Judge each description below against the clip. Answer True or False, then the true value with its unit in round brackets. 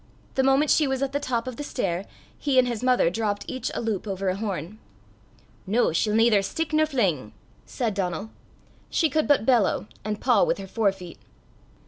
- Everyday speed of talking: False (210 wpm)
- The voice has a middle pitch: False (225 Hz)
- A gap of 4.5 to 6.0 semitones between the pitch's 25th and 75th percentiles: True (5.2 semitones)